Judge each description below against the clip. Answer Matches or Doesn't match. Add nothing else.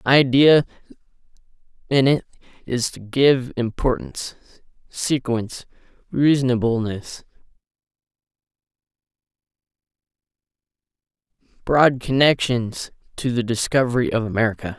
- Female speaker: Doesn't match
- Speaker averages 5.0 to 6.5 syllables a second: Doesn't match